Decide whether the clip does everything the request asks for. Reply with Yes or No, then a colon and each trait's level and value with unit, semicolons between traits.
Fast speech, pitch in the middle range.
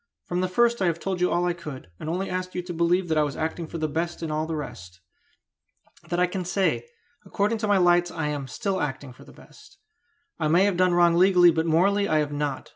Yes: fast, 250 wpm; medium, 175 Hz